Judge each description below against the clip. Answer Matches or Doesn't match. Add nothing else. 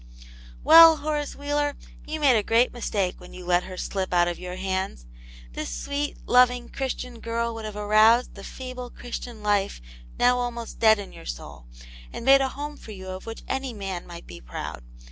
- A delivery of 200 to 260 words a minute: Doesn't match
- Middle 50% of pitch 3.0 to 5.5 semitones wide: Matches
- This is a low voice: Doesn't match